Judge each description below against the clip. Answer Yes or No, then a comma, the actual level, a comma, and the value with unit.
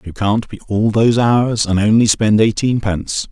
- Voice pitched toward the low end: Yes, low, 110 Hz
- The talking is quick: No, average, 180 wpm